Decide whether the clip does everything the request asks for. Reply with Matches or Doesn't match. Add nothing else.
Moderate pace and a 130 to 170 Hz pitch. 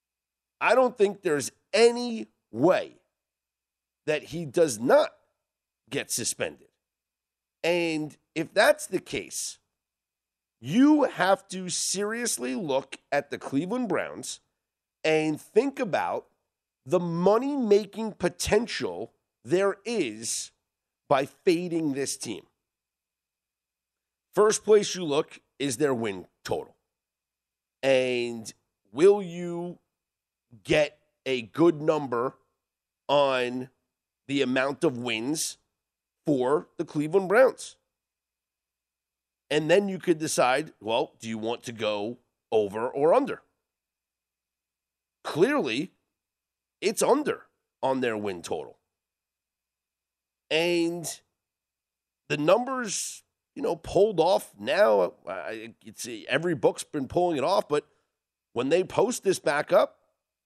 Doesn't match